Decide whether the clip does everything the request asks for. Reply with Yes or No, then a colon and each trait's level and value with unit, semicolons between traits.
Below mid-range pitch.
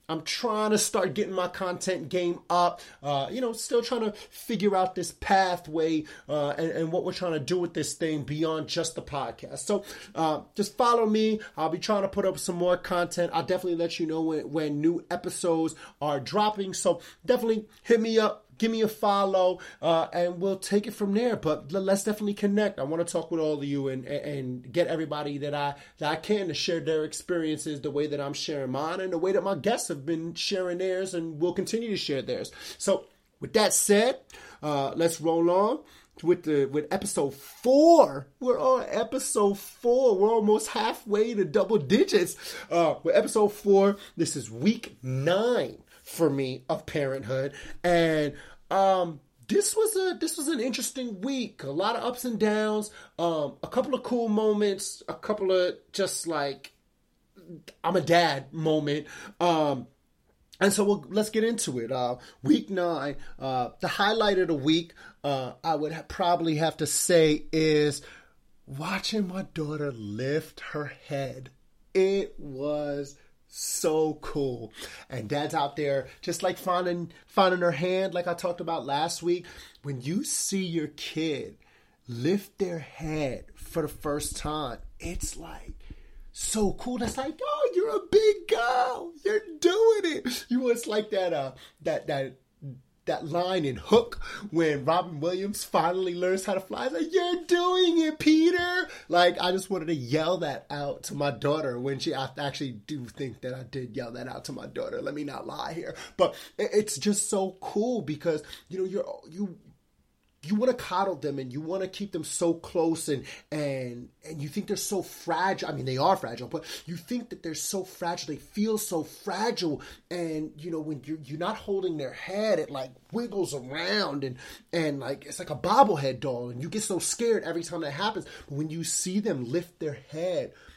No: medium, 175 Hz